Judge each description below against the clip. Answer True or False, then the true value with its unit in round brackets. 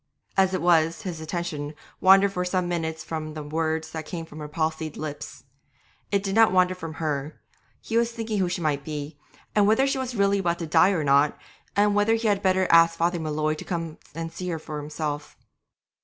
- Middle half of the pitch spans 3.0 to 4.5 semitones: True (3.7 semitones)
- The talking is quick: True (210 wpm)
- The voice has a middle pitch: True (165 Hz)